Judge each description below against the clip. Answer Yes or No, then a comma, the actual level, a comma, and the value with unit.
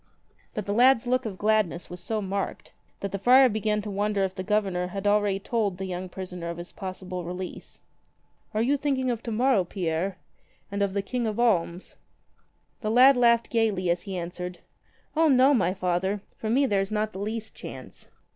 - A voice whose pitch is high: Yes, high, 205 Hz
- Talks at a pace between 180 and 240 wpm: Yes, average, 195 wpm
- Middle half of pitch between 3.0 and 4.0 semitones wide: Yes, average, 3.6 semitones